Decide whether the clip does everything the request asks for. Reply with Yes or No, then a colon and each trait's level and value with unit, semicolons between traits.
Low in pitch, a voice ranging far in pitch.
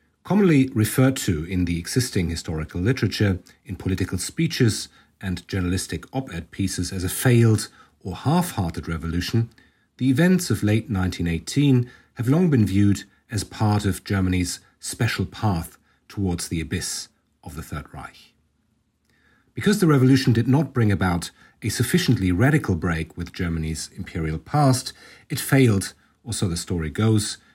Yes: low, 100 Hz; wide, 6.3 semitones